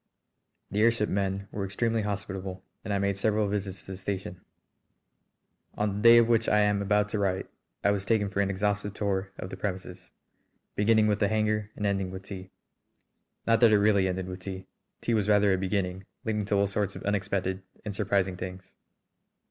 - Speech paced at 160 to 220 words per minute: Yes, average, 195 wpm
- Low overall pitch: Yes, low, 100 Hz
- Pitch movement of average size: No, narrow, 1.7 semitones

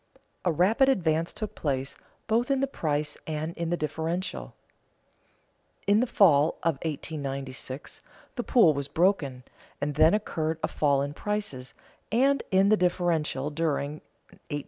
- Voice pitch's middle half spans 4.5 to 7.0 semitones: Yes, average, 5.2 semitones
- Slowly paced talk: No, average, 145 wpm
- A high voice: No, medium, 160 Hz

